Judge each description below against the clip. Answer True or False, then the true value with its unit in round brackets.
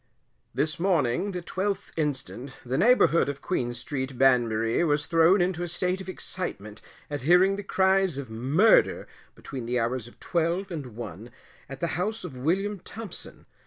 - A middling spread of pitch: False (6.6 semitones)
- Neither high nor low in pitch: True (160 Hz)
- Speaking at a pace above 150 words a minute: True (160 wpm)